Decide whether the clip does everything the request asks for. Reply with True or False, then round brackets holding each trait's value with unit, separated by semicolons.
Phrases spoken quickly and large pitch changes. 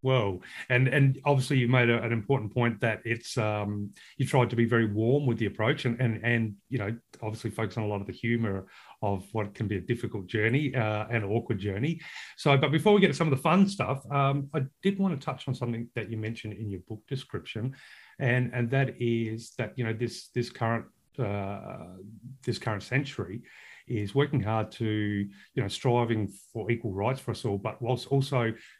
False (215 wpm; 3.3 semitones)